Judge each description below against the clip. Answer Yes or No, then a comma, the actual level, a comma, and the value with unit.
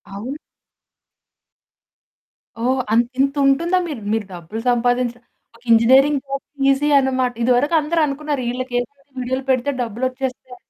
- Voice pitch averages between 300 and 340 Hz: No, very high, 255 Hz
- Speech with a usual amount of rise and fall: No, narrow, 2.2 semitones